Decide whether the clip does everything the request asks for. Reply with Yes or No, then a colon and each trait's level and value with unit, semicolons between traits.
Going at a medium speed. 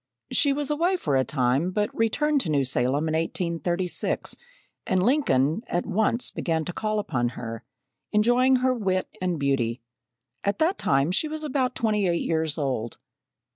Yes: average, 165 wpm